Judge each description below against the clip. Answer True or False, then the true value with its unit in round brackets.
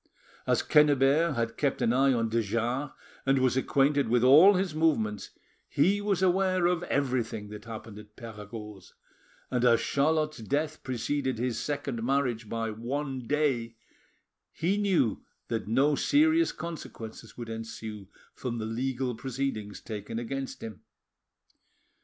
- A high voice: False (130 Hz)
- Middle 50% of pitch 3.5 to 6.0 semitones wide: True (4.6 semitones)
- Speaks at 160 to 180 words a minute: False (140 wpm)